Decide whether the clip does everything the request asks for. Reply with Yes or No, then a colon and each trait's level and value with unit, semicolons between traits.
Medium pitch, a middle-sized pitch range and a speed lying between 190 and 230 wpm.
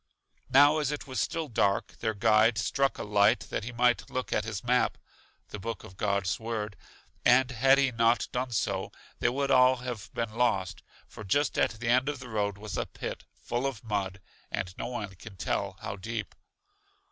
No: low, 115 Hz; average, 3.6 semitones; average, 195 wpm